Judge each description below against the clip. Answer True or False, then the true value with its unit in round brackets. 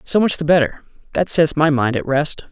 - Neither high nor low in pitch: True (155 Hz)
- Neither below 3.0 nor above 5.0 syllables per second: False (5.2 syllables/s)